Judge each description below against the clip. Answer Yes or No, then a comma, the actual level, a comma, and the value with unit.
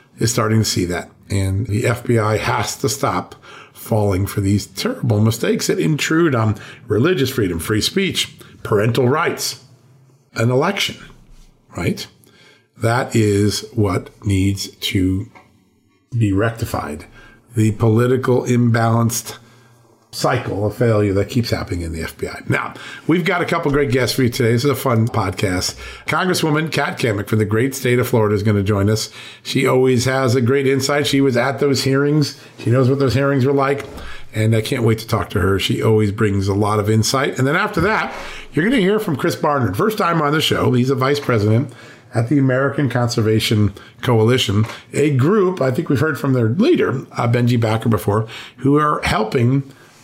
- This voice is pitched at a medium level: No, low, 120 Hz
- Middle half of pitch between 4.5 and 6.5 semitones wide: No, average, 4.1 semitones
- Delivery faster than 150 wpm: Yes, average, 180 wpm